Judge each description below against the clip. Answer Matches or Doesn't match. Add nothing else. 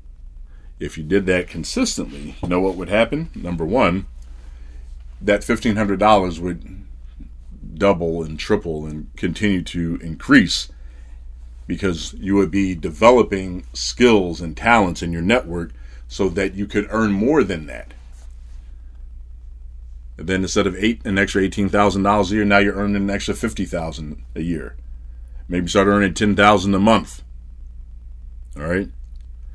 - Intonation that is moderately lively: Doesn't match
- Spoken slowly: Doesn't match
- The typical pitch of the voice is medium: Doesn't match